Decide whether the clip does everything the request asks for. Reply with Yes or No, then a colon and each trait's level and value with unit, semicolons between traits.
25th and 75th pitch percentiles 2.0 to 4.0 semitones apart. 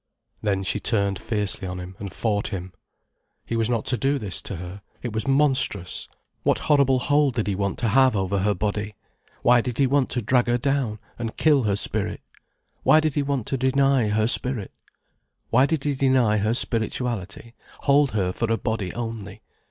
No: average, 4.6 semitones